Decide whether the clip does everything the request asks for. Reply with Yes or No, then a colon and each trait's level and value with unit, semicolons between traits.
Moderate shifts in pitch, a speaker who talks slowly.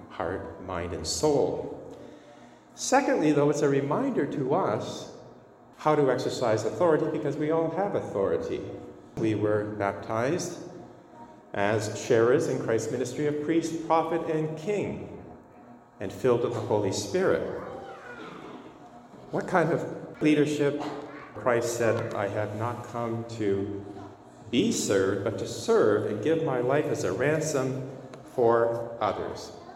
No: wide, 6.4 semitones; slow, 130 wpm